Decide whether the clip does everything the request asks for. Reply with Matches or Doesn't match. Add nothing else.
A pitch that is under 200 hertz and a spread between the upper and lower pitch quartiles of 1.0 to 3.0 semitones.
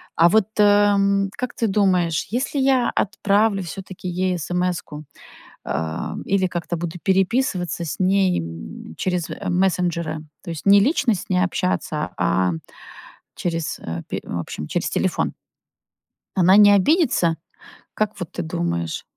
Doesn't match